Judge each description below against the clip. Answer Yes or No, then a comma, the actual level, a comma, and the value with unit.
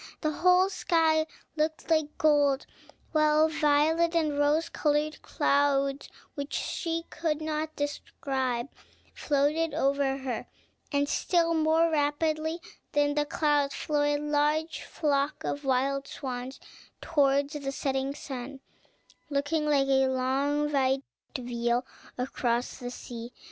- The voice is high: Yes, very high, 290 Hz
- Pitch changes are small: Yes, narrow, 2.3 semitones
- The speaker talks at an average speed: No, slow, 120 wpm